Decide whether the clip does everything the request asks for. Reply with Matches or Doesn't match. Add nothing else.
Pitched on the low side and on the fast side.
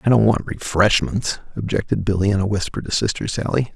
Doesn't match